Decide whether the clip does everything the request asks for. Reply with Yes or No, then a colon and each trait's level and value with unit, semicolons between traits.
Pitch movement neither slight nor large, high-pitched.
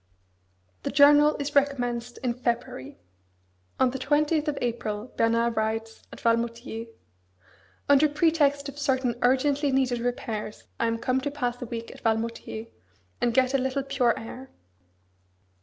Yes: average, 3.3 semitones; very high, 250 Hz